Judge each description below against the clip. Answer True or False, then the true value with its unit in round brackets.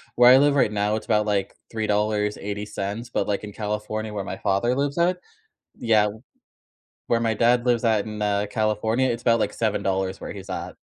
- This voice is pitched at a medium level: False (110 Hz)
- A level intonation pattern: True (2.2 semitones)